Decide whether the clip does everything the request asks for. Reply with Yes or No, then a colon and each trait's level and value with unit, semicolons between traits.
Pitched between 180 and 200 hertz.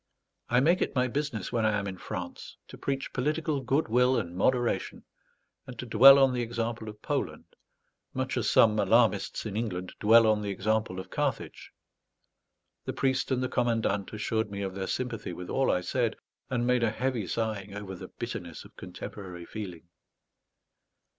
No: low, 110 Hz